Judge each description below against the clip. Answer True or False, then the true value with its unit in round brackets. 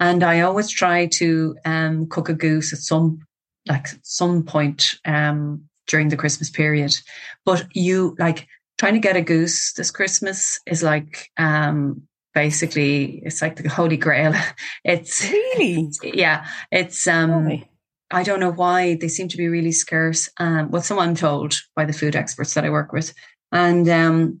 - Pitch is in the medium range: True (160 Hz)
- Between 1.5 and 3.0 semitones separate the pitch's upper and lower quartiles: True (2.4 semitones)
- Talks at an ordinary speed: True (170 wpm)